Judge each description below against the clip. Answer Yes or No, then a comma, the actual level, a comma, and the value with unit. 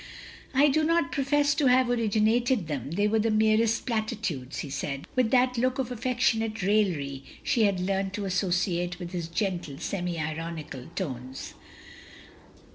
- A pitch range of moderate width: No, wide, 6.2 semitones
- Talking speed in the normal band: Yes, average, 160 wpm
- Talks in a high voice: Yes, high, 205 Hz